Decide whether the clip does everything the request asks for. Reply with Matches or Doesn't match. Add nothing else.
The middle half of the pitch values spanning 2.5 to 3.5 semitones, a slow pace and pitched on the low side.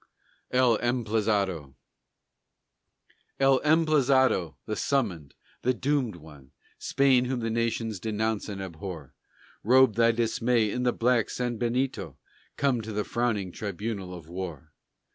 Doesn't match